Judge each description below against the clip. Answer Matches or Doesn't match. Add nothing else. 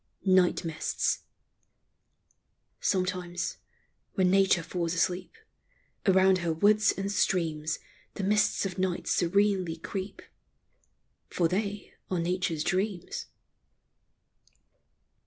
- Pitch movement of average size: Doesn't match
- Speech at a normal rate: Doesn't match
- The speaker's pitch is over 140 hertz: Matches